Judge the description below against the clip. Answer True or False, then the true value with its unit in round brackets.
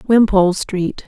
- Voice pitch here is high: True (195 Hz)